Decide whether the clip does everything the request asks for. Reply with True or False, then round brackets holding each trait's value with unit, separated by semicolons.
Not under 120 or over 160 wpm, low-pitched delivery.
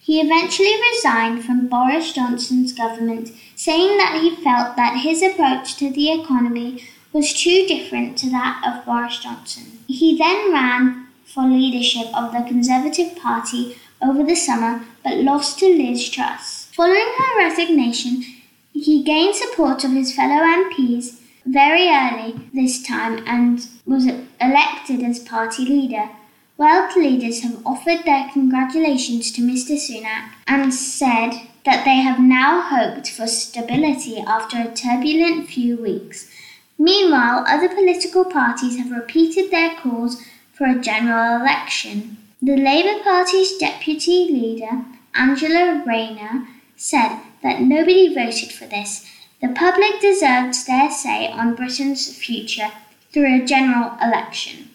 False (135 wpm; 260 Hz)